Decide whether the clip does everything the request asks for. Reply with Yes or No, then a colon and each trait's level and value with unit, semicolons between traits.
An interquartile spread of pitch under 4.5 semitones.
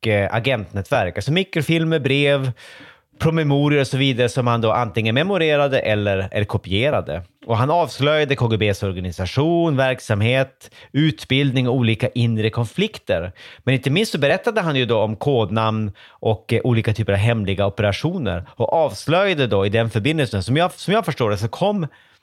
No: average, 4.9 semitones